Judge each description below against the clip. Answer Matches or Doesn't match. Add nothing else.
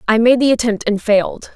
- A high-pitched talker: Matches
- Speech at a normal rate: Doesn't match